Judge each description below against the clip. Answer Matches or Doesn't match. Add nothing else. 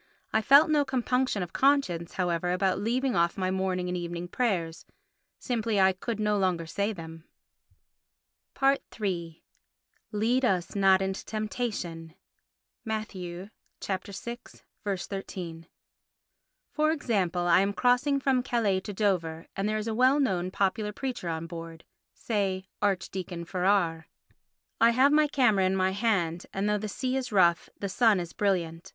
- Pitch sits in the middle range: Doesn't match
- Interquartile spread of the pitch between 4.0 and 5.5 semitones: Matches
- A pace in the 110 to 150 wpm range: Matches